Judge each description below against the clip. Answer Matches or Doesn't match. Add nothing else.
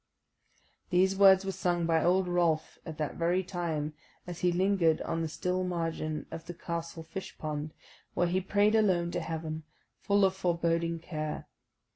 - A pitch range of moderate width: Doesn't match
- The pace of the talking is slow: Doesn't match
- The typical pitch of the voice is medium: Matches